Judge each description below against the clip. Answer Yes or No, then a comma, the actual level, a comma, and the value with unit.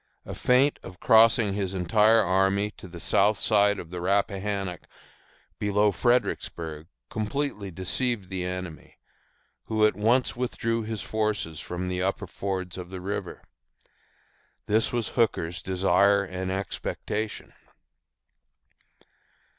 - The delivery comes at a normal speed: No, slow, 120 wpm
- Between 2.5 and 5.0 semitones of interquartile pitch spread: Yes, average, 2.9 semitones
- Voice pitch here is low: Yes, low, 100 Hz